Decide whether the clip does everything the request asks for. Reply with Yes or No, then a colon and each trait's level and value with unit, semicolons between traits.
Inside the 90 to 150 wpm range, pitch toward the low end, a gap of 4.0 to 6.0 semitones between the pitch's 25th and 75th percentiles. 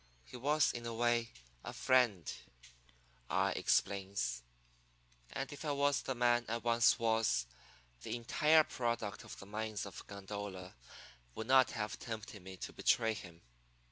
No: average, 145 wpm; low, 115 Hz; average, 3.3 semitones